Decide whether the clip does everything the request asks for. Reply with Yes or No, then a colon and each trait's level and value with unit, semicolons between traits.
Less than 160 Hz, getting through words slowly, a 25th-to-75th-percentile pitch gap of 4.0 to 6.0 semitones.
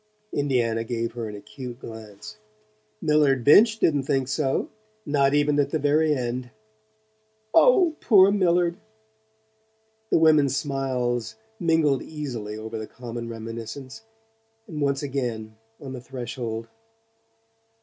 Yes: low, 135 Hz; slow, 120 wpm; average, 4.3 semitones